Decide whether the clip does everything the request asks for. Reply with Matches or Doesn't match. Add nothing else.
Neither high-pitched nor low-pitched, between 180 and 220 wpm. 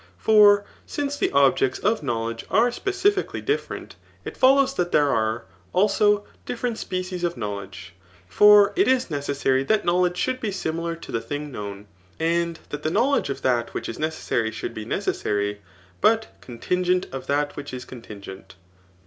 Doesn't match